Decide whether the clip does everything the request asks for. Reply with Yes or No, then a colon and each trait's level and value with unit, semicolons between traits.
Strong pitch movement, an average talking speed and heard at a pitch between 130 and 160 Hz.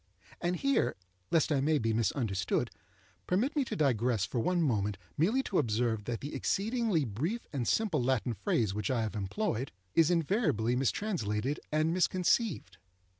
Yes: wide, 8.2 semitones; average, 155 wpm; medium, 140 Hz